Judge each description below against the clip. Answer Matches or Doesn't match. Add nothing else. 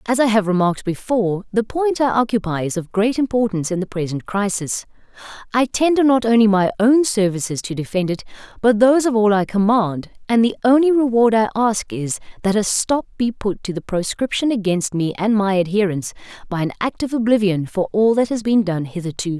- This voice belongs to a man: Doesn't match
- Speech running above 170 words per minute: Matches